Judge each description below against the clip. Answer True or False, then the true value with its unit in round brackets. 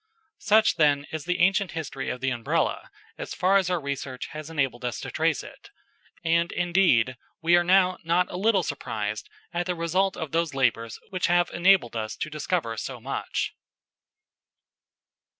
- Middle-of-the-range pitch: True (165 Hz)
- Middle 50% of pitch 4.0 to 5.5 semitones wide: True (5.2 semitones)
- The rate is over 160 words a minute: True (170 wpm)